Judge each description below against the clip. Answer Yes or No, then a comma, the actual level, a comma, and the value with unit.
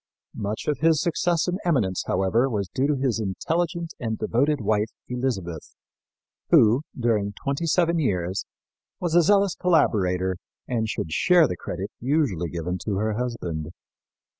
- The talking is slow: No, average, 145 wpm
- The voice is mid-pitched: No, low, 120 Hz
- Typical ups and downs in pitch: No, wide, 8.6 semitones